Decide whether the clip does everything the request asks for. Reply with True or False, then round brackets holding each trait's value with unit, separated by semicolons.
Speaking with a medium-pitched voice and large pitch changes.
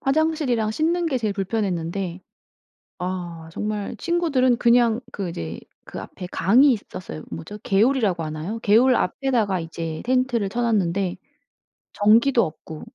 False (210 Hz; 5.9 semitones)